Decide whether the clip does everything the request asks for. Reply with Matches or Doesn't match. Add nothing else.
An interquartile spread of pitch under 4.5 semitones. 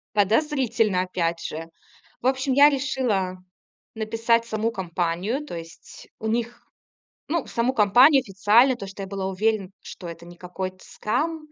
Doesn't match